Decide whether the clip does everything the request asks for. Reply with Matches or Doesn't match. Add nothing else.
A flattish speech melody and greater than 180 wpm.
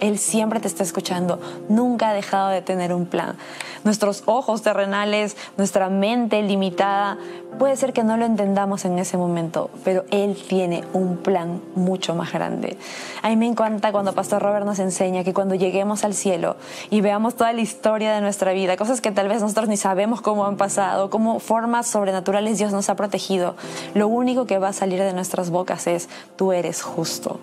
Matches